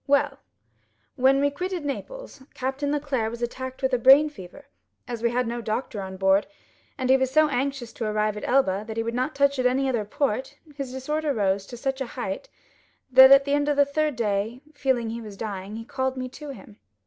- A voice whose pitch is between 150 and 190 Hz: No, very high, 260 Hz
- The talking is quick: Yes, fast, 220 wpm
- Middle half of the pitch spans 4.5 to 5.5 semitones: No, average, 3.7 semitones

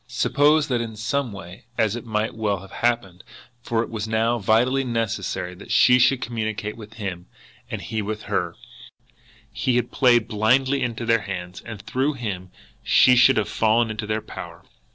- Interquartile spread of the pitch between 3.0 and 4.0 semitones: No, narrow, 2.5 semitones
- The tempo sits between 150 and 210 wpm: Yes, average, 175 wpm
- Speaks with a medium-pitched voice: No, low, 115 Hz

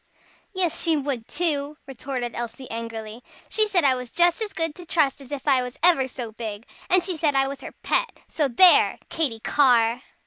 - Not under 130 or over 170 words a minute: No, average, 200 wpm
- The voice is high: Yes, very high, 275 Hz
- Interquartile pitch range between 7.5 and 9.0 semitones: No, average, 5.3 semitones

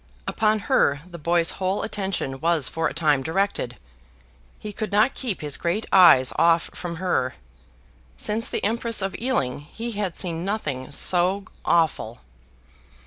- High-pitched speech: No, medium, 175 Hz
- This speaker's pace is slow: No, average, 145 wpm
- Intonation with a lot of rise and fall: No, average, 4.8 semitones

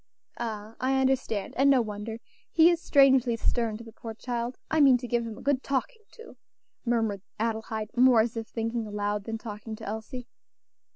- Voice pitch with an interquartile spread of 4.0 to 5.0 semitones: No, average, 3.0 semitones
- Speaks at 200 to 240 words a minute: No, average, 185 wpm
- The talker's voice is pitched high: Yes, high, 230 Hz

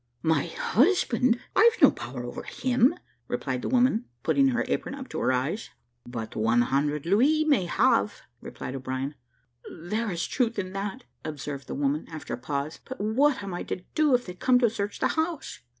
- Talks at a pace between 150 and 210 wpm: Yes, average, 185 wpm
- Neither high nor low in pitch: No, high, 205 Hz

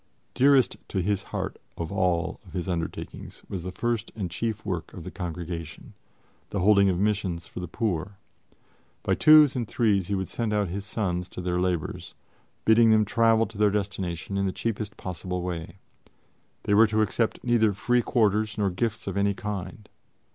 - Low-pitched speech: Yes, low, 100 Hz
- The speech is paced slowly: No, average, 175 wpm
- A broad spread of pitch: No, average, 3.4 semitones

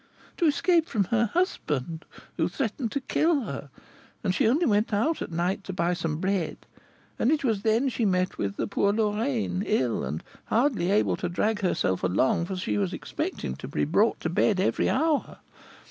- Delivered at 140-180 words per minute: No, average, 190 wpm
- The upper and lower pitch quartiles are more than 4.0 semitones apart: Yes, wide, 5.6 semitones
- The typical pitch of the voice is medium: No, high, 200 Hz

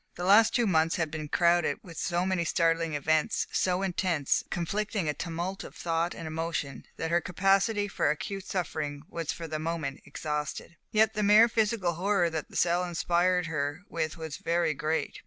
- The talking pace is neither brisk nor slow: Yes, average, 180 wpm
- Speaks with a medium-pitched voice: Yes, medium, 170 Hz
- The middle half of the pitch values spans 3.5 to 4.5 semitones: No, average, 3.0 semitones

